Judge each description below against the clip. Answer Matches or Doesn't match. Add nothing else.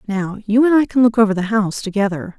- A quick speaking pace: Matches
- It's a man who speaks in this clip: Doesn't match